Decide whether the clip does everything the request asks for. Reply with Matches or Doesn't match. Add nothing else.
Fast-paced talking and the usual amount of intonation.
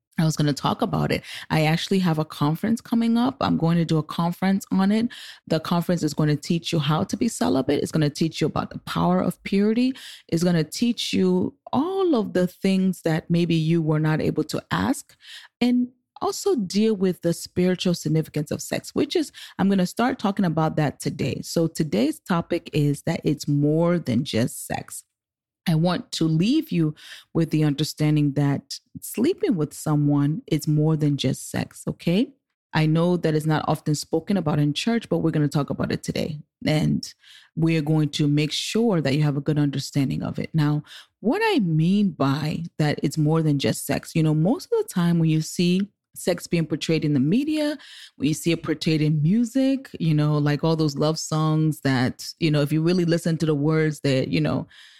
Matches